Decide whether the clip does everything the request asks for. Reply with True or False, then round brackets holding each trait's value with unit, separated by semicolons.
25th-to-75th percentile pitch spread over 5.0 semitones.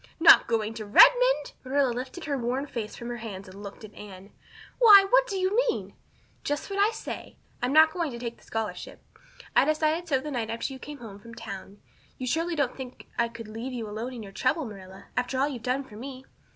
True (5.5 semitones)